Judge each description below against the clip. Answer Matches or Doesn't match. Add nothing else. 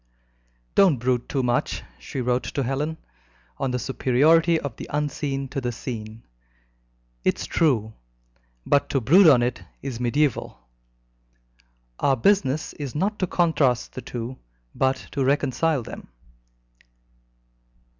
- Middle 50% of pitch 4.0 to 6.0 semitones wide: Doesn't match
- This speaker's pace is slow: Matches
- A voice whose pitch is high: Doesn't match